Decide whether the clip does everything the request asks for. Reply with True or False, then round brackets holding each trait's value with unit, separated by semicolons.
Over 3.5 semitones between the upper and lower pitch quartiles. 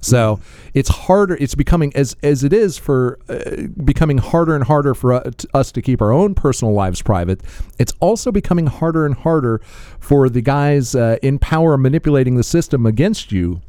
True (4.6 semitones)